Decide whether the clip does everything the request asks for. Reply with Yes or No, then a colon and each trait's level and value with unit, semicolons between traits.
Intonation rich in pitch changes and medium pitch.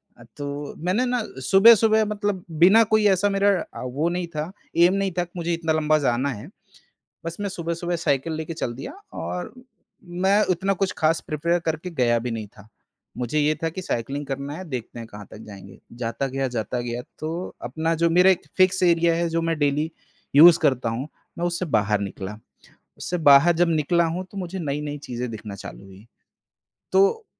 Yes: wide, 5.8 semitones; medium, 160 Hz